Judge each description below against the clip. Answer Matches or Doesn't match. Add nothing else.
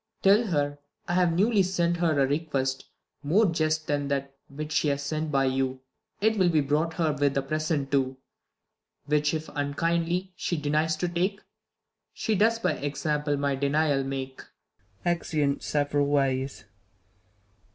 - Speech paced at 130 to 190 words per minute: Matches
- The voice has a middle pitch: Matches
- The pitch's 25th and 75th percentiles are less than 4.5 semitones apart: Matches